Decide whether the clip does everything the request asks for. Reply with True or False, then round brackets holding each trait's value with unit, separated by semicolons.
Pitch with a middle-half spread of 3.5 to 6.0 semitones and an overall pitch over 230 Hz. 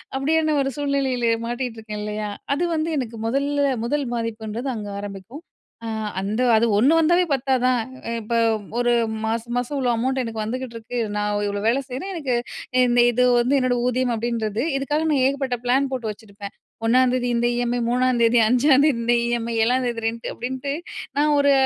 False (3.0 semitones; 245 Hz)